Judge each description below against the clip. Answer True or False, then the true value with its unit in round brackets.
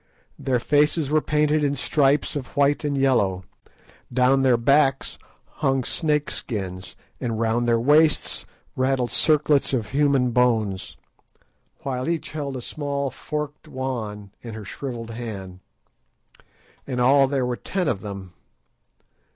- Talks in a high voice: False (130 Hz)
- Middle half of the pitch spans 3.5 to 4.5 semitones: True (3.8 semitones)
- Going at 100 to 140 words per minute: True (135 wpm)